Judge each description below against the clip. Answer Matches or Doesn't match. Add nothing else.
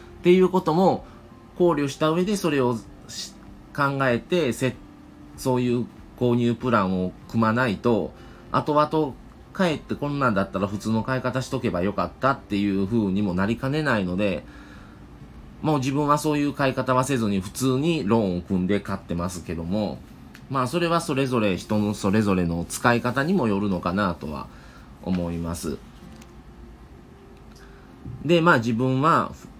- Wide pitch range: Matches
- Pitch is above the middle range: Doesn't match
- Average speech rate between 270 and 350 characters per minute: Matches